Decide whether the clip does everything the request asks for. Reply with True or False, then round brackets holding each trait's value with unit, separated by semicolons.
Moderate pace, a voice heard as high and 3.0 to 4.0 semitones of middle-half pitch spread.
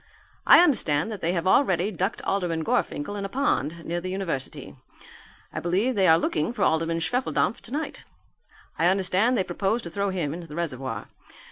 False (175 wpm; 180 Hz; 3.6 semitones)